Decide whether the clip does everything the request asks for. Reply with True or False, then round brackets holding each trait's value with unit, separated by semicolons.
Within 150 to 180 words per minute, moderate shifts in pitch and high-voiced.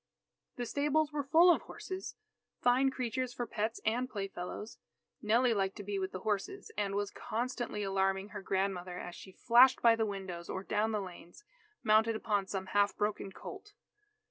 True (170 wpm; 4.2 semitones; 215 Hz)